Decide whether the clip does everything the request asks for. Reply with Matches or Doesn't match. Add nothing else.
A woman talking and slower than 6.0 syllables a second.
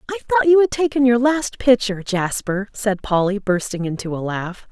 Matches